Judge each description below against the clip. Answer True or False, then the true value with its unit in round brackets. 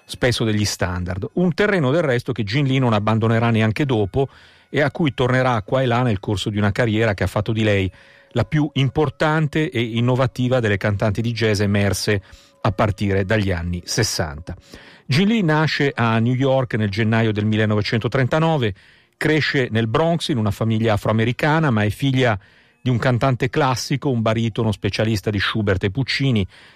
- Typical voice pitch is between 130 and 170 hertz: False (115 Hz)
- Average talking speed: False (175 wpm)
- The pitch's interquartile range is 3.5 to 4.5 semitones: True (4.1 semitones)